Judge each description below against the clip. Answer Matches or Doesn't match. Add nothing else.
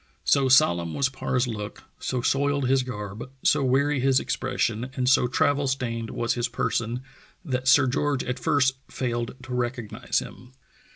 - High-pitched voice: Doesn't match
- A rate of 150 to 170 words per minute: Matches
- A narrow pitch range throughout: Matches